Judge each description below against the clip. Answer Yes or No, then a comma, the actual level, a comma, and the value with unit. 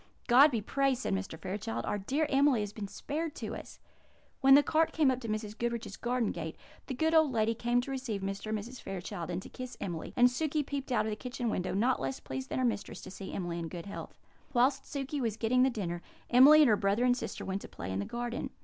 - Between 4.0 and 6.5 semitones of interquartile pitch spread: Yes, average, 5.1 semitones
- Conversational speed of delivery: No, fast, 250 wpm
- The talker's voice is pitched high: Yes, high, 235 Hz